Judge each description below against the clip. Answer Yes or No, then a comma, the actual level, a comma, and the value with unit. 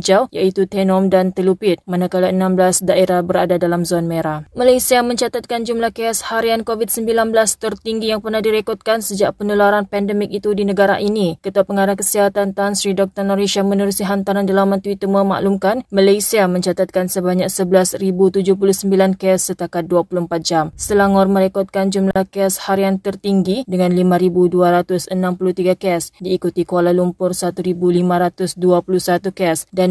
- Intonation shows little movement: Yes, narrow, 1.8 semitones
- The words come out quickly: No, average, 130 wpm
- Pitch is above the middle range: Yes, high, 195 Hz